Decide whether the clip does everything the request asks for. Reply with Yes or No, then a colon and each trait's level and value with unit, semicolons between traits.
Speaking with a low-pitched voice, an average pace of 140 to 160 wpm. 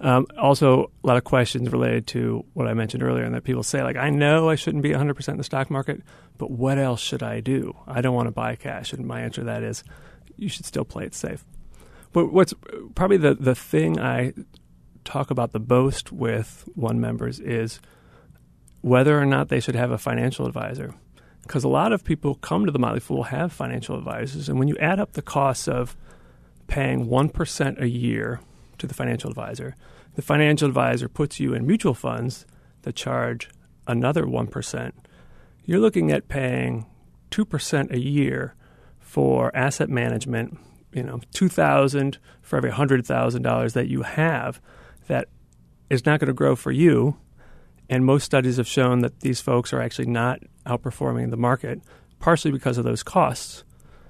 No: low, 125 Hz; average, 180 wpm